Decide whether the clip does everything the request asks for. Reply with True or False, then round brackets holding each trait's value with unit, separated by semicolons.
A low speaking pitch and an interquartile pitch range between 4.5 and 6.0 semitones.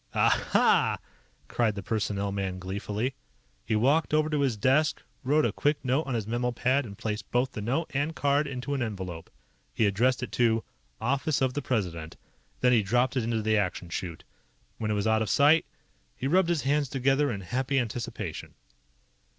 True (125 Hz; 4.8 semitones)